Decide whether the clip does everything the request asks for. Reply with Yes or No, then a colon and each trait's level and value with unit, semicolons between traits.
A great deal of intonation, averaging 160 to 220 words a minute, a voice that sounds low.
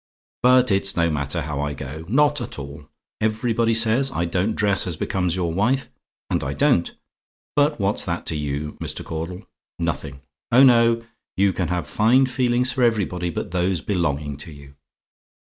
Yes: wide, 6.9 semitones; average, 170 wpm; very low, 95 Hz